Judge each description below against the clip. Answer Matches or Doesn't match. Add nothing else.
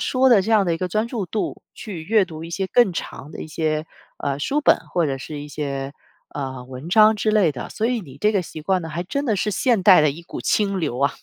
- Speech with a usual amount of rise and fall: Doesn't match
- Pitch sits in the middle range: Matches